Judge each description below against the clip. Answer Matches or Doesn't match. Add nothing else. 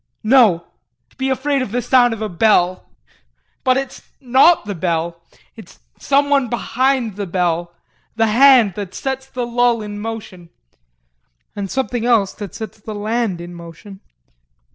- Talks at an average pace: Matches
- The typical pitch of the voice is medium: Doesn't match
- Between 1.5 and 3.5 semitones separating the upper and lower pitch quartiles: Doesn't match